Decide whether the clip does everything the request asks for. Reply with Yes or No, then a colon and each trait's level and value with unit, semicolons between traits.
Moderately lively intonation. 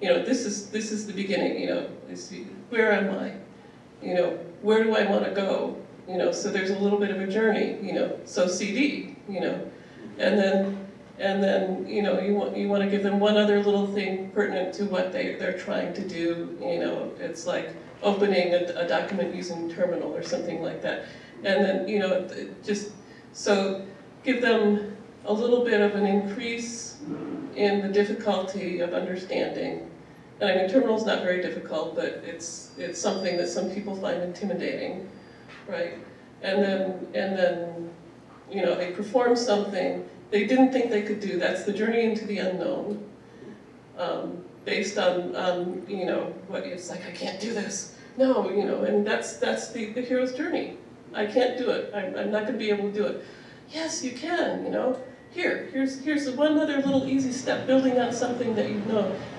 Yes: average, 3.8 semitones